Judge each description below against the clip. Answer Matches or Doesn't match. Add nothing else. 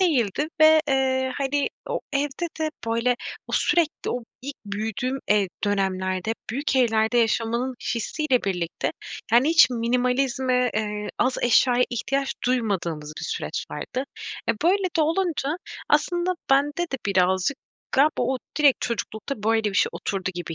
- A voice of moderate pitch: Doesn't match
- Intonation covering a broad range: Doesn't match